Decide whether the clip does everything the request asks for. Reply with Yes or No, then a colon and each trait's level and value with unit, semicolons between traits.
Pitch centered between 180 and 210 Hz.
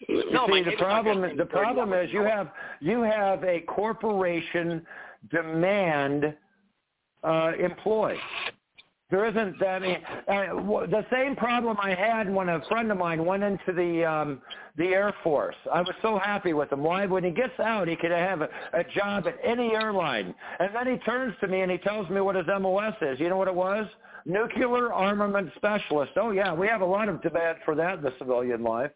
Yes: high, 190 Hz